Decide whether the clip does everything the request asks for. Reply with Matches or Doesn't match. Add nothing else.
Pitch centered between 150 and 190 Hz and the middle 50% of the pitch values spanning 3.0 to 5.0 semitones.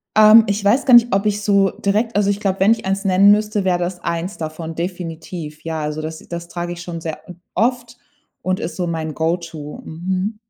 Matches